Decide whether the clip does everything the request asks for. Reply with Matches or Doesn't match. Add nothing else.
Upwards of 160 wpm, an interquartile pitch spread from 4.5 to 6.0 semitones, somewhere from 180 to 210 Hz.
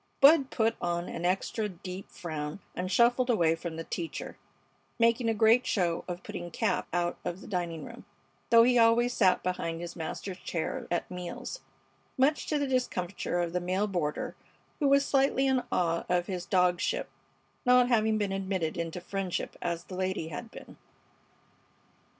Matches